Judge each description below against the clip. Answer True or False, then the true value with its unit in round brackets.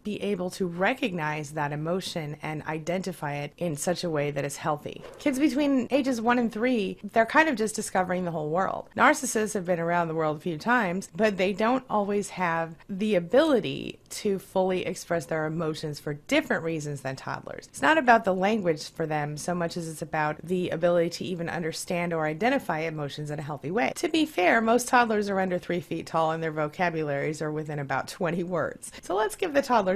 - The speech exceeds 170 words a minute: True (205 wpm)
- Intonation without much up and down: False (5.6 semitones)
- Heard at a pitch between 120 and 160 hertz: False (175 Hz)